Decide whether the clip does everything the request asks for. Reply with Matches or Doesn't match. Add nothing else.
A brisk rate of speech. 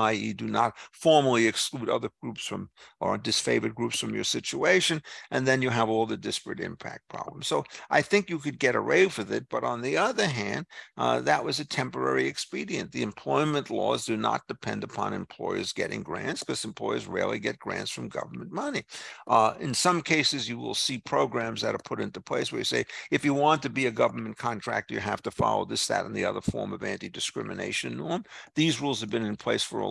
Matches